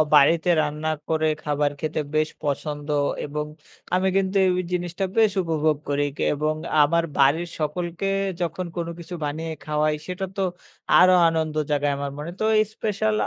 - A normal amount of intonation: Yes, average, 3.1 semitones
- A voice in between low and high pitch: Yes, medium, 160 Hz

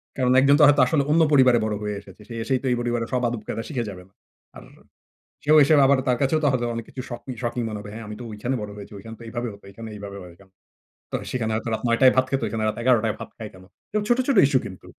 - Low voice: Yes, low, 120 Hz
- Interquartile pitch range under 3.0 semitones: No, average, 3.5 semitones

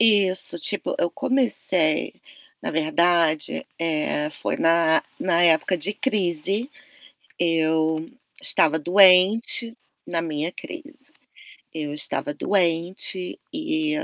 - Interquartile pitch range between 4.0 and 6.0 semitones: Yes, average, 4.4 semitones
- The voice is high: No, medium, 175 Hz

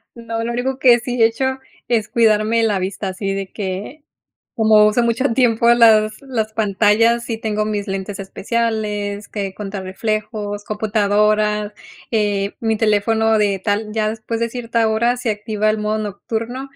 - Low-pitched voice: No, high, 215 Hz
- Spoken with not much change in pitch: Yes, narrow, 1.9 semitones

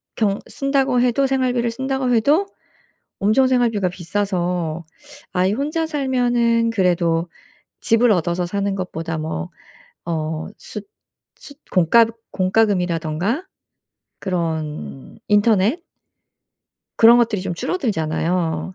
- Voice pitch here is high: Yes, high, 205 Hz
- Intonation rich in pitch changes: Yes, wide, 5.8 semitones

